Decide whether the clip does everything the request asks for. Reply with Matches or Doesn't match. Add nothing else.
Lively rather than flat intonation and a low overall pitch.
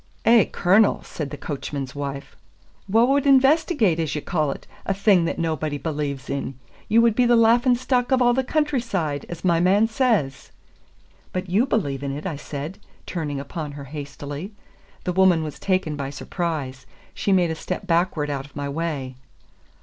Doesn't match